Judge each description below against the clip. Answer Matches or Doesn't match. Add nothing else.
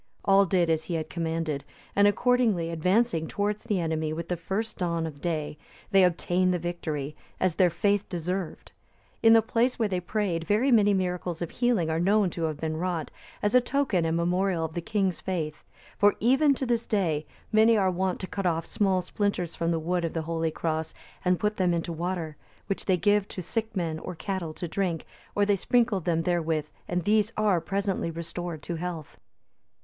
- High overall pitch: Doesn't match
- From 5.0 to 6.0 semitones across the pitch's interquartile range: Doesn't match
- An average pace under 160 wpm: Doesn't match